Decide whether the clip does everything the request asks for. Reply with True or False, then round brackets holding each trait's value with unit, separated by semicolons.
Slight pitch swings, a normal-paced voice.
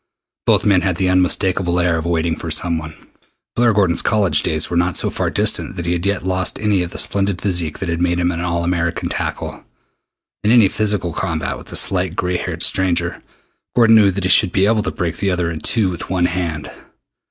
False (2.3 semitones; 220 wpm)